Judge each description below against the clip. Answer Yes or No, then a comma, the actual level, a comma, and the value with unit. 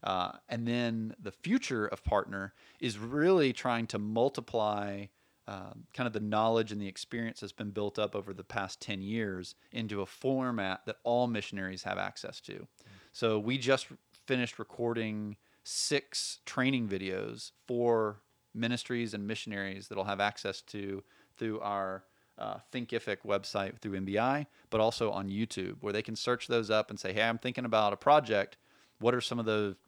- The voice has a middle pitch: No, low, 110 Hz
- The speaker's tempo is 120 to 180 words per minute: Yes, average, 170 wpm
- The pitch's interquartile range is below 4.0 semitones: Yes, average, 3.1 semitones